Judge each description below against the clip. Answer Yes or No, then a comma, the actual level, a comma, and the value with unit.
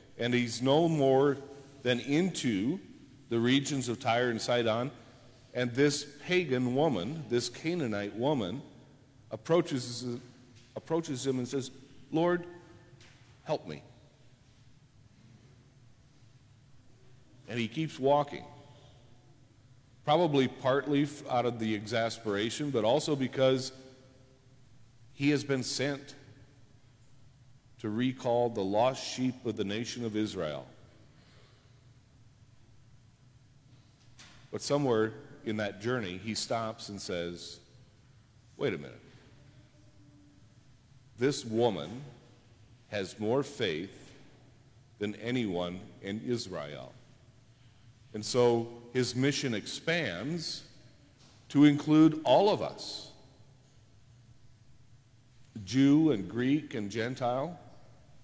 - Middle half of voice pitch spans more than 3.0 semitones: No, narrow, 2.5 semitones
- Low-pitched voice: Yes, low, 125 Hz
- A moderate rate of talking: No, slow, 95 wpm